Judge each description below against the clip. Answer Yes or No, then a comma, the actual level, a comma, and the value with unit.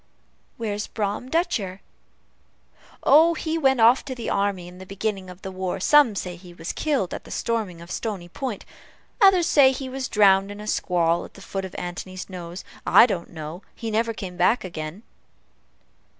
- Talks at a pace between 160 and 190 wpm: Yes, average, 180 wpm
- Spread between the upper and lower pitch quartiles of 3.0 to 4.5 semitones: No, average, 4.9 semitones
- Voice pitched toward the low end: No, high, 200 Hz